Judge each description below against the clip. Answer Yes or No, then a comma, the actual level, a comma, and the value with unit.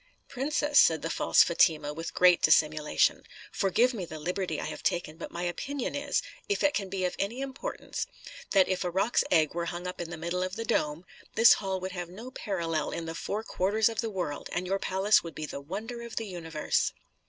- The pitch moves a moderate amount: Yes, average, 4.8 semitones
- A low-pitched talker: No, medium, 185 Hz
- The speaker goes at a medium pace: No, fast, 220 wpm